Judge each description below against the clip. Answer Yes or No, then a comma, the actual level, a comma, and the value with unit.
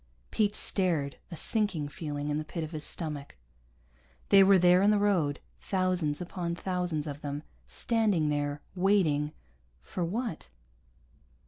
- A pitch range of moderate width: Yes, average, 4.5 semitones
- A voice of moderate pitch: Yes, medium, 170 Hz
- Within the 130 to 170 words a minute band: Yes, average, 140 wpm